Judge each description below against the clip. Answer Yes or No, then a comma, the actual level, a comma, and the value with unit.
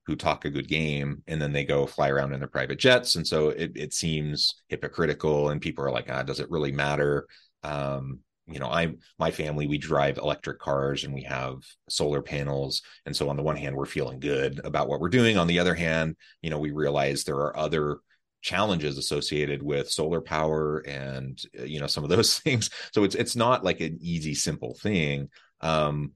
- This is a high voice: No, very low, 75 Hz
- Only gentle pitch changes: Yes, narrow, 2.0 semitones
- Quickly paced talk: Yes, fast, 210 wpm